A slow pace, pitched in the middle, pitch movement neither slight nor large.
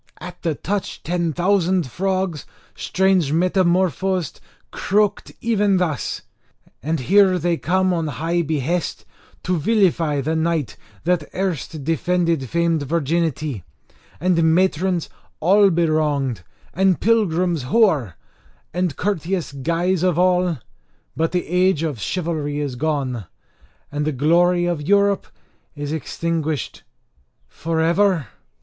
Yes: slow, 115 wpm; medium, 170 Hz; average, 3.1 semitones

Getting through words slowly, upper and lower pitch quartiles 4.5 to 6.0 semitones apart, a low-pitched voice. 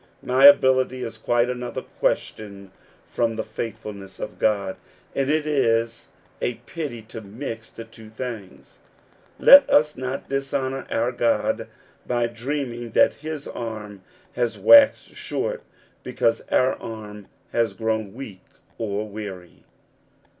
No: slow, 125 wpm; average, 3.3 semitones; low, 115 Hz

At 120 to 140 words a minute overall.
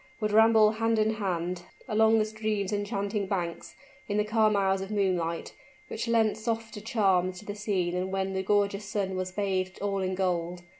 No: average, 185 wpm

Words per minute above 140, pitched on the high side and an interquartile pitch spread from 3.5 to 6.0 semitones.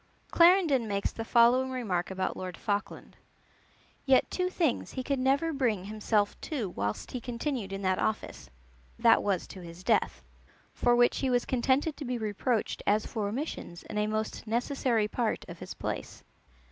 Yes: average, 170 wpm; high, 235 Hz; average, 4.4 semitones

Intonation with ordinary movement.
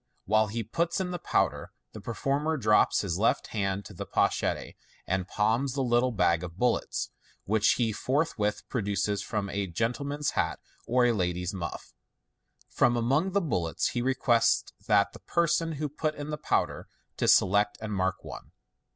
No: wide, 5.8 semitones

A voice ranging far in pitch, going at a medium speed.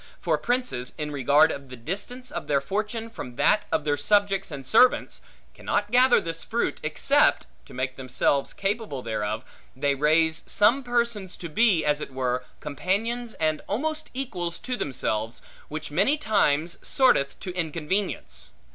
Yes: wide, 7.7 semitones; average, 155 wpm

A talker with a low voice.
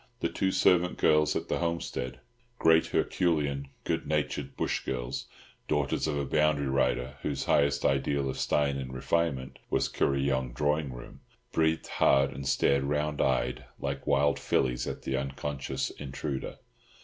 Yes: very low, 70 Hz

